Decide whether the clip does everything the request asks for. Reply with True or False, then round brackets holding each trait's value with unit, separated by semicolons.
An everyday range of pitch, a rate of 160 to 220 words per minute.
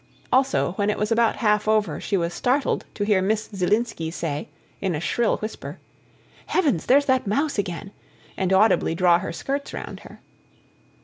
True (4.9 semitones; 170 wpm)